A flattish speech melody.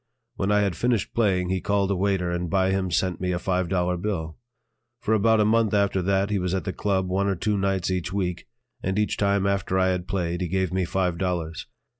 Yes: narrow, 1.7 semitones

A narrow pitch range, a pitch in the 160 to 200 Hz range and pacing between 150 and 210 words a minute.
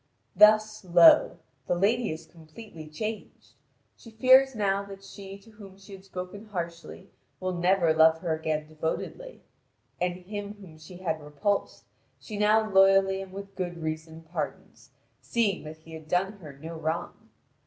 No: average, 4.1 semitones; medium, 185 Hz; average, 155 wpm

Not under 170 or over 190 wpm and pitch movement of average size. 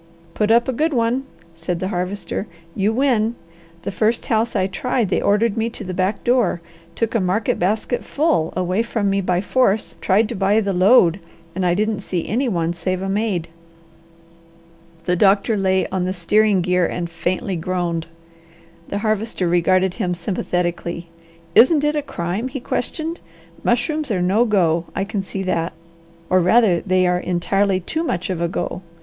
Yes: average, 175 wpm; average, 4.0 semitones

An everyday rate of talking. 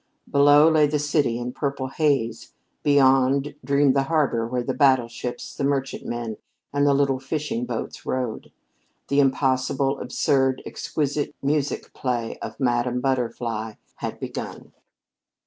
No: slow, 130 wpm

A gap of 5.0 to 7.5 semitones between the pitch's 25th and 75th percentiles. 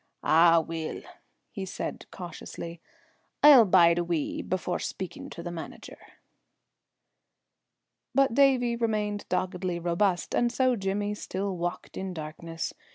No: average, 3.6 semitones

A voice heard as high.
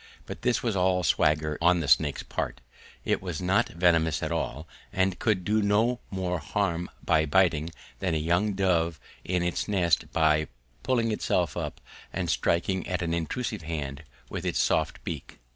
No: very low, 90 Hz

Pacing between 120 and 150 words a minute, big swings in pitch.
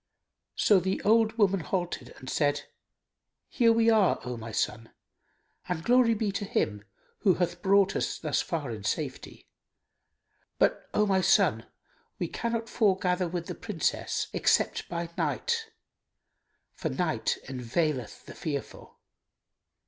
Yes: slow, 135 wpm; wide, 6.5 semitones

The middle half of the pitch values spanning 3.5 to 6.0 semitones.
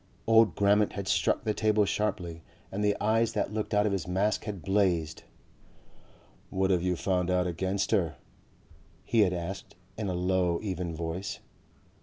No: average, 2.7 semitones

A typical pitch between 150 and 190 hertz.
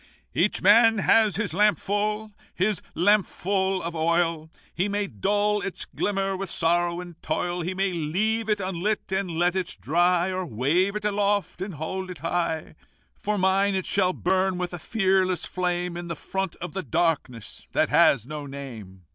Yes: medium, 185 Hz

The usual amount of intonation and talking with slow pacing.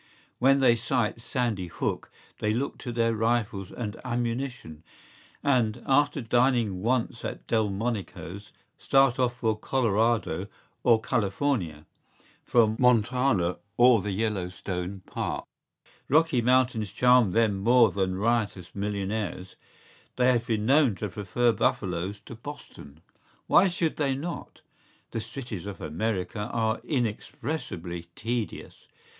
Yes: average, 4.0 semitones; slow, 125 wpm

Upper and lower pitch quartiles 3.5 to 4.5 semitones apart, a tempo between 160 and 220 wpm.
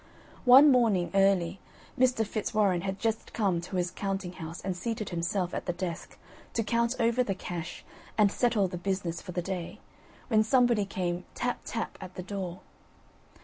Yes: average, 4.0 semitones; average, 170 wpm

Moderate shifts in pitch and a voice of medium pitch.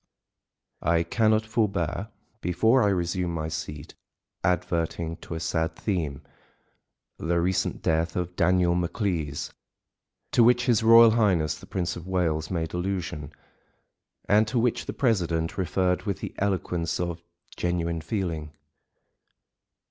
No: average, 3.3 semitones; very low, 90 Hz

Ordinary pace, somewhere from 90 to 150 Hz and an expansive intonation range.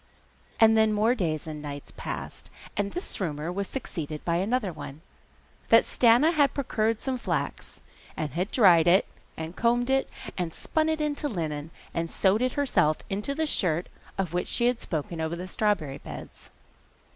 No: average, 170 wpm; high, 195 Hz; wide, 7.0 semitones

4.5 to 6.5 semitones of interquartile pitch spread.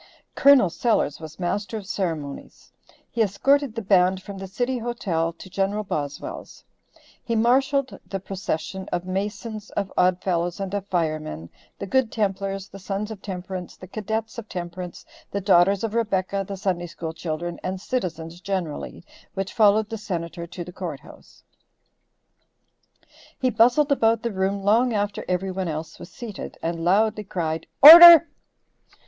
No: average, 3.9 semitones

